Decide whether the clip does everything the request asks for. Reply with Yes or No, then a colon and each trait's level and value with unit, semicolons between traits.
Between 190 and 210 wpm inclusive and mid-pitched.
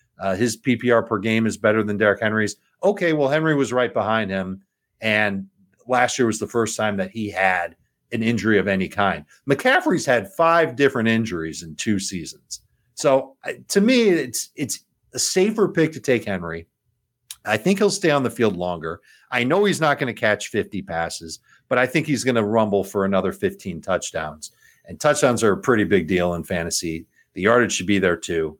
No: average, 200 wpm; low, 110 Hz